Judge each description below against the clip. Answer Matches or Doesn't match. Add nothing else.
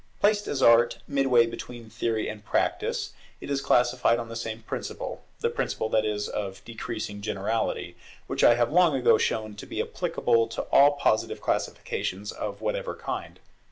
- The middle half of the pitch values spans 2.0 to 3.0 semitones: Matches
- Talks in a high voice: Doesn't match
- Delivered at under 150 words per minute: Doesn't match